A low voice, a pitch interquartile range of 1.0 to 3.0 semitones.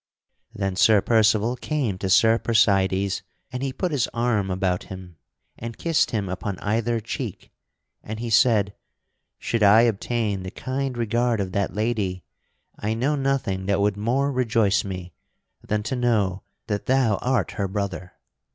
No: low, 110 Hz; average, 3.4 semitones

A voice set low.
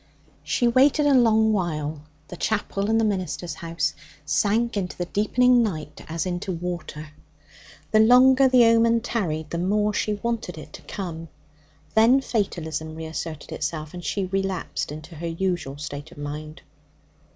No: medium, 185 Hz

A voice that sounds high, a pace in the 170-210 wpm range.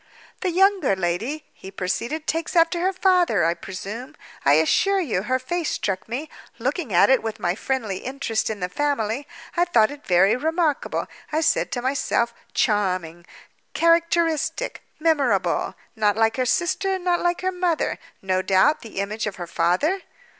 No: very high, 255 Hz; average, 160 wpm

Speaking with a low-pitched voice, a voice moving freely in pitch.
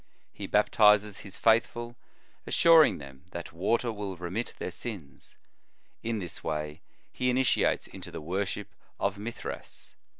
No: low, 105 Hz; average, 5.0 semitones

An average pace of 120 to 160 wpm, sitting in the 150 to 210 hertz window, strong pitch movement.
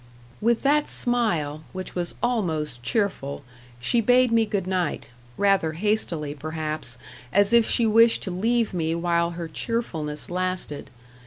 Yes: average, 140 wpm; medium, 185 Hz; wide, 6.2 semitones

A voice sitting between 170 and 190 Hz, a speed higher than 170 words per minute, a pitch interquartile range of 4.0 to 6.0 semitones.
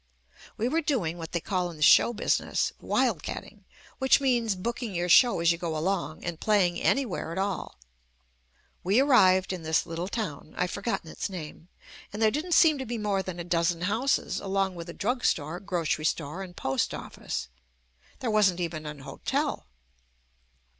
Yes: medium, 185 Hz; average, 185 wpm; average, 4.8 semitones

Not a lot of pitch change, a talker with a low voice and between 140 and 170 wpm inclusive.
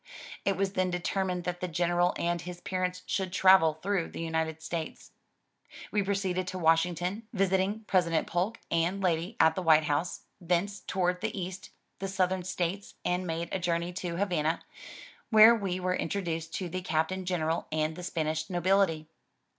No: narrow, 2.3 semitones; medium, 180 Hz; average, 165 wpm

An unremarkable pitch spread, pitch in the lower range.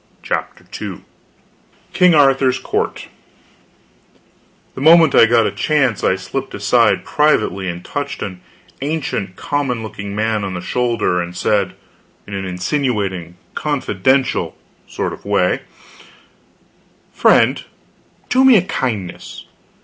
No: wide, 7.0 semitones; low, 115 Hz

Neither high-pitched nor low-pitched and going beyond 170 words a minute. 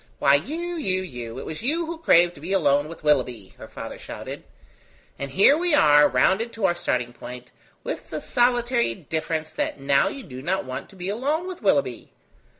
Yes: medium, 175 Hz; average, 195 wpm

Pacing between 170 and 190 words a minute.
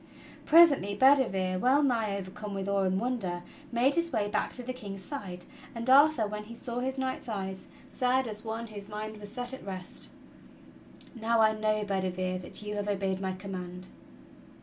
Yes: average, 180 wpm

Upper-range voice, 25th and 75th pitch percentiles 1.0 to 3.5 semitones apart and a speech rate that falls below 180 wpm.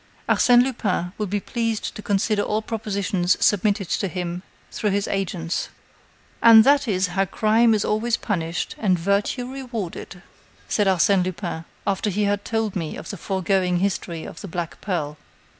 Yes: high, 200 Hz; average, 3.2 semitones; average, 160 wpm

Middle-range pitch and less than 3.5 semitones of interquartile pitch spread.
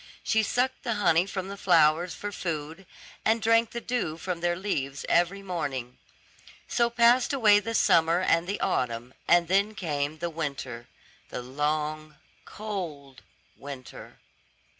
No: medium, 175 Hz; wide, 5.6 semitones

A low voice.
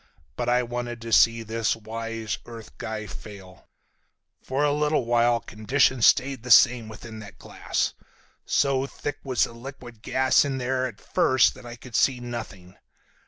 Yes: low, 120 Hz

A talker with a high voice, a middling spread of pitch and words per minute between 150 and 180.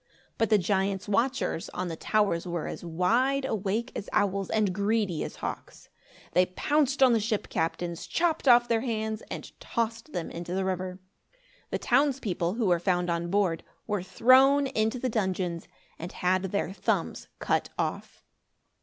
Yes: high, 205 Hz; average, 4.4 semitones; average, 165 wpm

